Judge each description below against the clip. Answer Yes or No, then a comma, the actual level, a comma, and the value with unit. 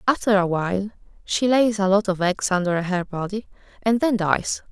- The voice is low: No, high, 200 Hz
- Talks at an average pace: Yes, average, 190 wpm